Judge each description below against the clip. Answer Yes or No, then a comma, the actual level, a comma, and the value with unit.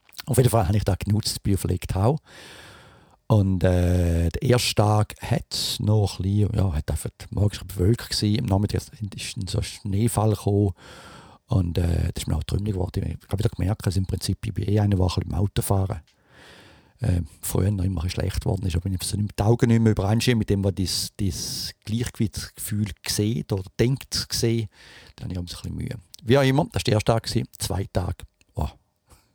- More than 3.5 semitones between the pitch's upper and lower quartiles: No, average, 3.1 semitones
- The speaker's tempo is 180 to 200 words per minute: Yes, average, 195 wpm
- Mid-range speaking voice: No, low, 100 Hz